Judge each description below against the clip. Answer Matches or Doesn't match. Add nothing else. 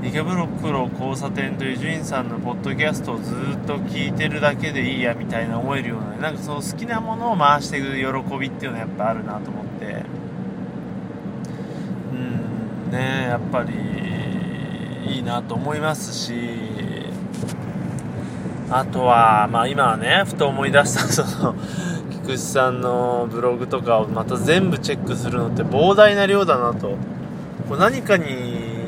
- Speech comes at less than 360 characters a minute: Matches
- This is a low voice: Matches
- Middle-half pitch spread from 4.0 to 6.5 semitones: Matches